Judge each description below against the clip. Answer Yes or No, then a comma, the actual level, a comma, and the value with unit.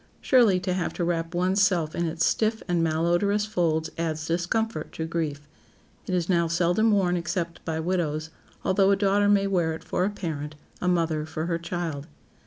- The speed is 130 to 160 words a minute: No, average, 190 wpm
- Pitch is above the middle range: No, medium, 175 Hz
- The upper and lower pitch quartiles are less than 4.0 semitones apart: Yes, average, 2.9 semitones